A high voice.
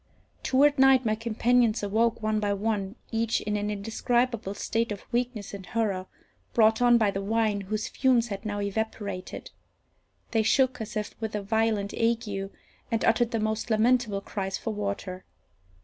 Yes: high, 220 Hz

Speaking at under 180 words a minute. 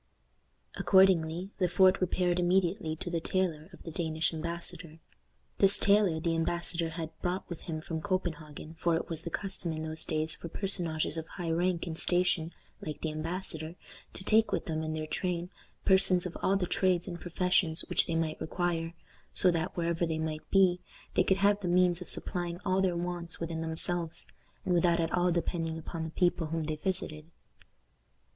No: average, 185 wpm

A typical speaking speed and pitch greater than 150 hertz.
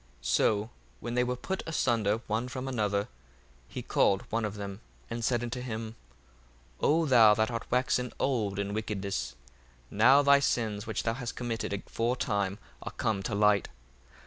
No: average, 165 wpm; low, 115 Hz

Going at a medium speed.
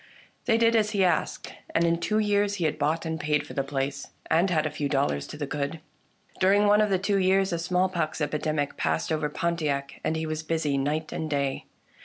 No: fast, 220 wpm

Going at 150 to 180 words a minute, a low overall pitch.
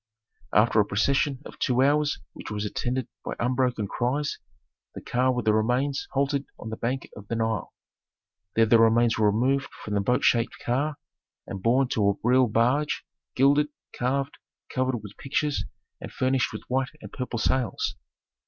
Yes: average, 170 wpm; low, 125 Hz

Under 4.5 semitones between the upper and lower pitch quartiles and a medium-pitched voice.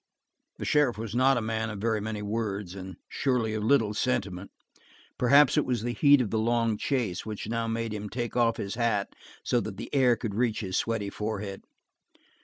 No: average, 2.7 semitones; low, 110 Hz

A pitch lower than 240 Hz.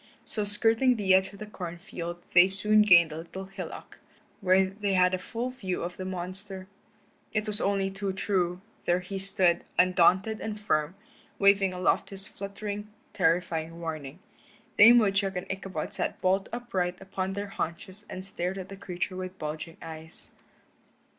Yes: high, 190 Hz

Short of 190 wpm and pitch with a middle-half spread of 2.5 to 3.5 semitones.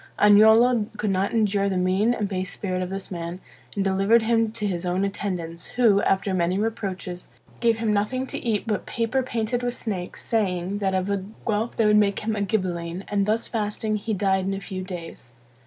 No: fast, 205 wpm; average, 2.9 semitones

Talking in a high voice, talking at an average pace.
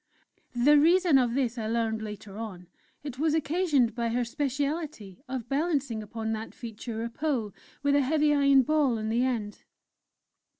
Yes: very high, 250 Hz; average, 165 wpm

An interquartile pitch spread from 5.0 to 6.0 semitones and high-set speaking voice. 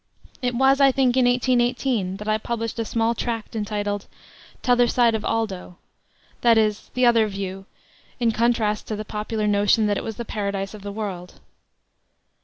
No: average, 2.7 semitones; high, 220 Hz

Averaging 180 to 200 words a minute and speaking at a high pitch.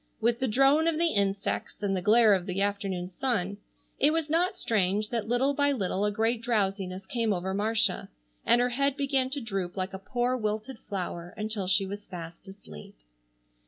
Yes: average, 190 wpm; high, 210 Hz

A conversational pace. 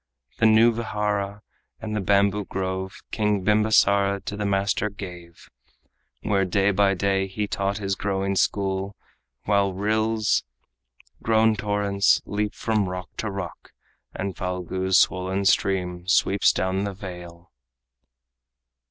No: slow, 125 wpm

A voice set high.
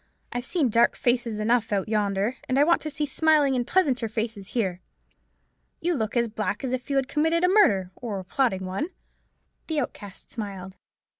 Yes: high, 240 Hz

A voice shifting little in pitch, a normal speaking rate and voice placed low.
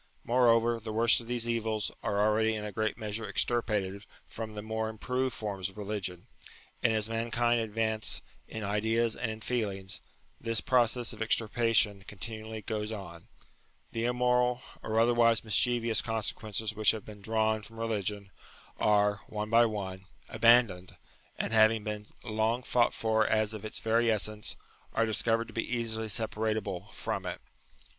Yes: narrow, 1.5 semitones; average, 165 wpm; low, 110 Hz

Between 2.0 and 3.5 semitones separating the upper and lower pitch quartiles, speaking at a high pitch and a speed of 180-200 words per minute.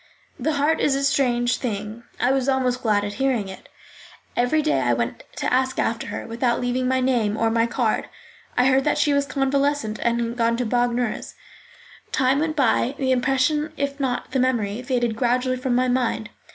Yes: narrow, 2.6 semitones; very high, 250 Hz; average, 190 wpm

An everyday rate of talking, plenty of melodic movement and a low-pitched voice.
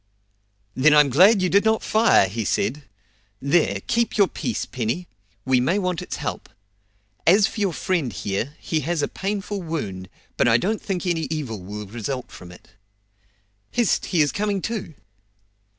No: average, 165 wpm; wide, 8.3 semitones; medium, 160 Hz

